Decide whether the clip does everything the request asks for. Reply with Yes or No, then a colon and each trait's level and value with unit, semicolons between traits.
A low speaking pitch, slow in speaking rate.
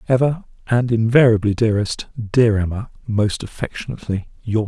Yes: low, 115 Hz; slow, 115 wpm